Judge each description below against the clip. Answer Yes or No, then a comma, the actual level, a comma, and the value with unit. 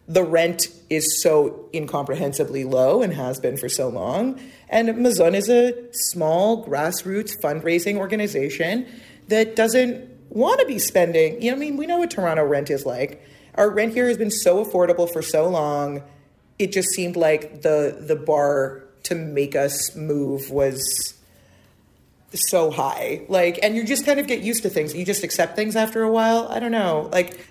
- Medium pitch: Yes, medium, 180 Hz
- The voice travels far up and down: Yes, wide, 6.8 semitones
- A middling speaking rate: Yes, average, 180 wpm